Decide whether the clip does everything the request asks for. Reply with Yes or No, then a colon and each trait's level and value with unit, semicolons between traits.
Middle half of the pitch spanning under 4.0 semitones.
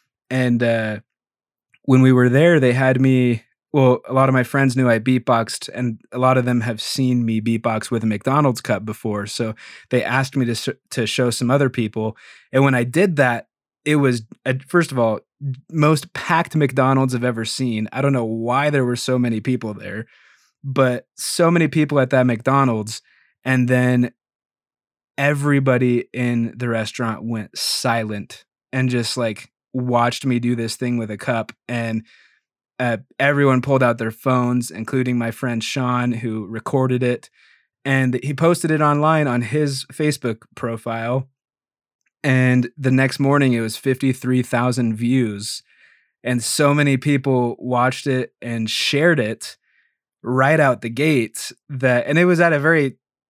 Yes: narrow, 2.4 semitones